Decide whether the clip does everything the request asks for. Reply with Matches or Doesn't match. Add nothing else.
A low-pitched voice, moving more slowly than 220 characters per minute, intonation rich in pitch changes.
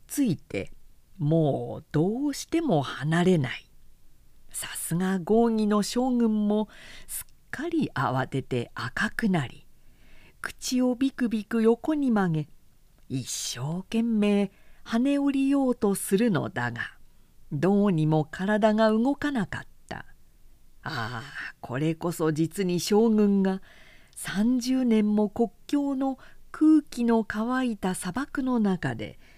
Doesn't match